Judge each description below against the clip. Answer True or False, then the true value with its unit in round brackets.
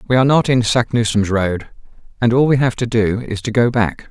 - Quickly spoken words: True (235 wpm)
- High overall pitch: False (115 Hz)